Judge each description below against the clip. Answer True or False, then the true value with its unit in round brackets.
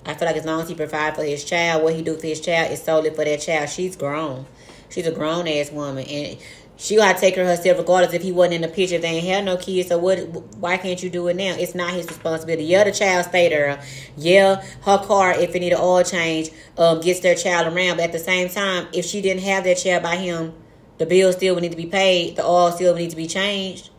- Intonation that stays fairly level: True (2.2 semitones)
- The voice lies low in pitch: False (175 Hz)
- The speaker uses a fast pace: True (275 wpm)